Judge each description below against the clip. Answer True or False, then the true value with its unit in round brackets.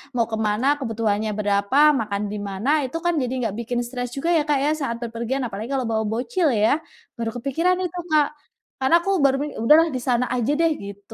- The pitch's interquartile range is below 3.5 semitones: False (4.0 semitones)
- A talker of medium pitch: False (240 Hz)